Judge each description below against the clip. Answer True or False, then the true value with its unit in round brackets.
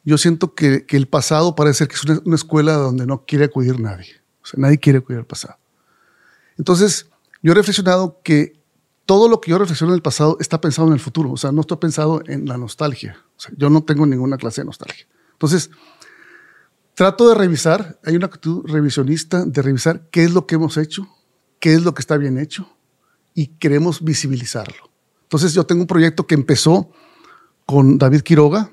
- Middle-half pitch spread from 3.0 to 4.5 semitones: True (3.5 semitones)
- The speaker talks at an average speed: False (200 wpm)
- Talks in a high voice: False (155 Hz)